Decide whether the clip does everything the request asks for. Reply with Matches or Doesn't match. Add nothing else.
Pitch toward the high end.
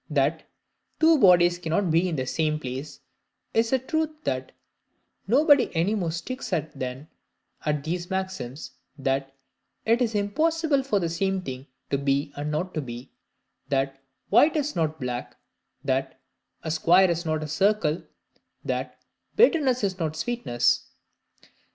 Doesn't match